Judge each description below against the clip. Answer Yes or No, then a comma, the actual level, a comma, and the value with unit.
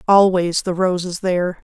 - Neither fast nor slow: Yes, average, 175 wpm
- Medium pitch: Yes, medium, 180 Hz